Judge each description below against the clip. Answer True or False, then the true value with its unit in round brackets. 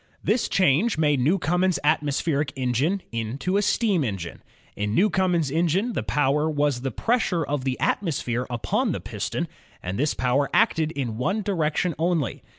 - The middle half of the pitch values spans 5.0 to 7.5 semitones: True (5.5 semitones)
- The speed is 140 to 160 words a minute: True (155 wpm)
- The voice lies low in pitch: False (150 Hz)